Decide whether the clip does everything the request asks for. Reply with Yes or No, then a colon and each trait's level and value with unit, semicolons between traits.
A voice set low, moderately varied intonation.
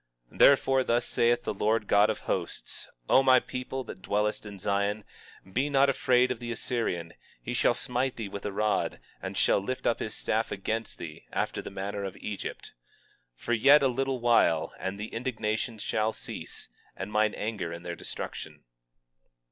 Yes: low, 110 Hz; average, 3.5 semitones